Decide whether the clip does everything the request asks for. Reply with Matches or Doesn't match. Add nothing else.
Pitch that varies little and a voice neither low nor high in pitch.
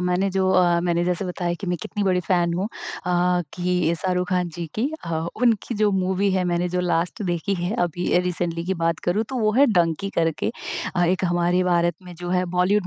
Matches